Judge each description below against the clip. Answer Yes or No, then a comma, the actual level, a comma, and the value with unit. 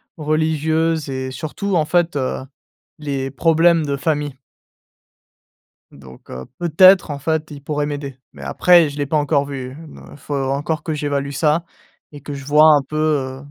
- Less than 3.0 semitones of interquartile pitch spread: Yes, narrow, 2.4 semitones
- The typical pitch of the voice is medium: Yes, medium, 150 Hz